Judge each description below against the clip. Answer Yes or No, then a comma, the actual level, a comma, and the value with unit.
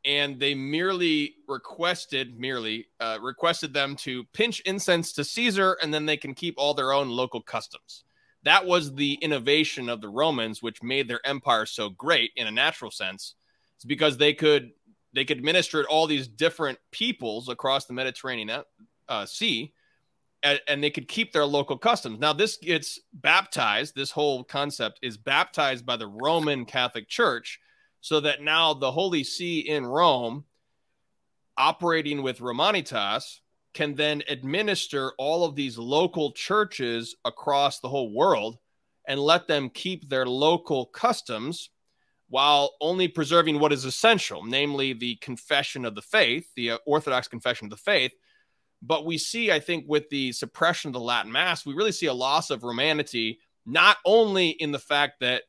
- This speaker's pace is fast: No, average, 165 wpm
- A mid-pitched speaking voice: Yes, medium, 145 Hz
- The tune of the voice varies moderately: Yes, average, 4.2 semitones